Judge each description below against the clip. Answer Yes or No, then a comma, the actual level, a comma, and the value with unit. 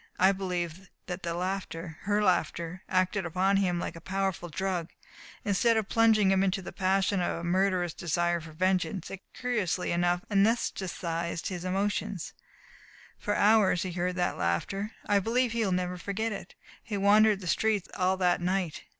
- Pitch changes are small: Yes, narrow, 2.3 semitones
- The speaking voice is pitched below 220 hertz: Yes, medium, 185 Hz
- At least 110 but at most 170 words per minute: Yes, average, 165 wpm